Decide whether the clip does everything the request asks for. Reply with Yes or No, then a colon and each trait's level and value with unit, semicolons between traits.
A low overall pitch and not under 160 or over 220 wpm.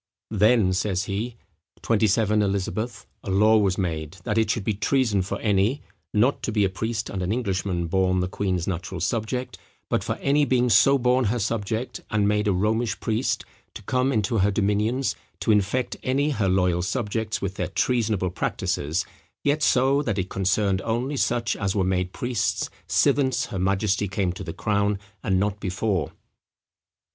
Yes: low, 105 Hz; average, 170 wpm